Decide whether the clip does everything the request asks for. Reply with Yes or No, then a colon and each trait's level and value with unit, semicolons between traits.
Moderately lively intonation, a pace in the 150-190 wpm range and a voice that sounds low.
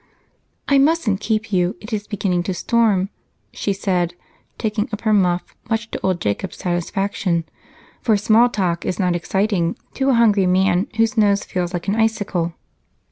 No: average, 3.3 semitones; average, 165 wpm; high, 200 Hz